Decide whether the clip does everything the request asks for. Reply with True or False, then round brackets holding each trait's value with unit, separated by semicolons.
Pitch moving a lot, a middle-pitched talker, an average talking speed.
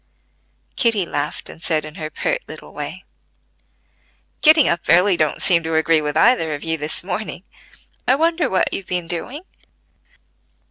True (6.5 semitones; 175 Hz; 155 wpm)